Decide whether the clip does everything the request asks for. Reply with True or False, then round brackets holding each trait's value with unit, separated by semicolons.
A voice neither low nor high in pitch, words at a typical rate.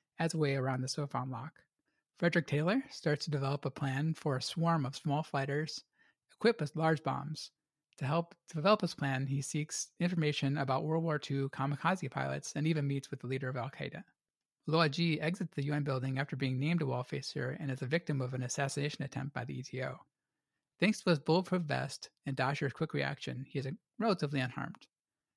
True (145 Hz; 195 wpm)